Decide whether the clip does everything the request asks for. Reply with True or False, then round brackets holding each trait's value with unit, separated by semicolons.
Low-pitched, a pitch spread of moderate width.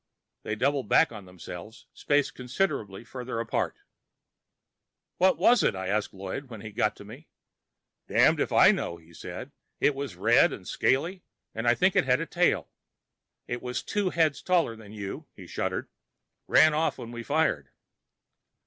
False (120 Hz; 6.1 semitones)